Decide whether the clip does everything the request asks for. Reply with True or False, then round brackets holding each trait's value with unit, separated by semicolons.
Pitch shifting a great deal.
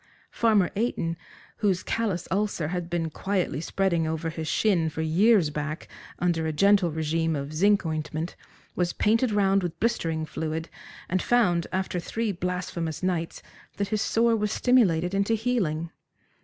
False (4.1 semitones)